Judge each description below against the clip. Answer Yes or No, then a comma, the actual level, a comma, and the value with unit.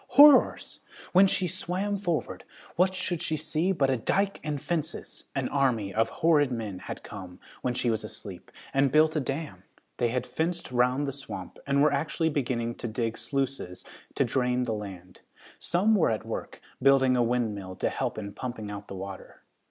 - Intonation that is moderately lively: No, wide, 5.8 semitones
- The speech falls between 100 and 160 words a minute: No, average, 185 wpm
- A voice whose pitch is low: Yes, low, 130 Hz